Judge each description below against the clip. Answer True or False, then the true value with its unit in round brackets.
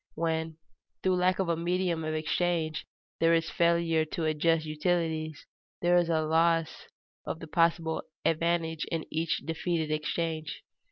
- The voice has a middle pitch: True (165 Hz)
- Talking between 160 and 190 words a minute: False (150 wpm)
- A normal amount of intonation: False (1.2 semitones)